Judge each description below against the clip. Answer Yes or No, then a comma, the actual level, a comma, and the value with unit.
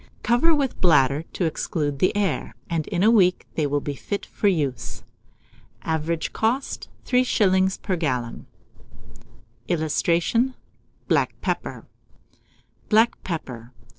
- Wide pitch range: Yes, wide, 6.4 semitones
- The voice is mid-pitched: Yes, medium, 175 Hz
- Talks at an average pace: No, slow, 115 wpm